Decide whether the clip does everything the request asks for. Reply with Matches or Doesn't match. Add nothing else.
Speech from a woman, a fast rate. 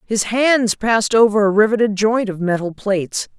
Doesn't match